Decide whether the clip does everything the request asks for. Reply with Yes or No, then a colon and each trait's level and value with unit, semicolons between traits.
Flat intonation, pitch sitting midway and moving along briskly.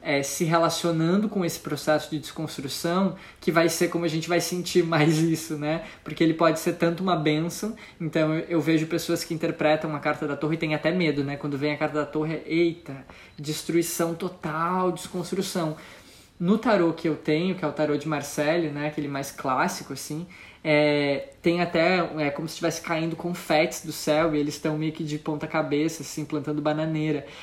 Yes: narrow, 1.9 semitones; medium, 160 Hz; fast, 195 wpm